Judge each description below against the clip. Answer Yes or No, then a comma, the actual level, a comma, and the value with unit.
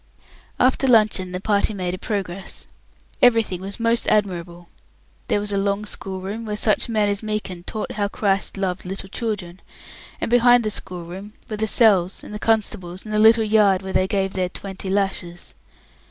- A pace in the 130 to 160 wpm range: No, average, 175 wpm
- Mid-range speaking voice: No, high, 200 Hz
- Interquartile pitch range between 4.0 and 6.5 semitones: No, narrow, 2.5 semitones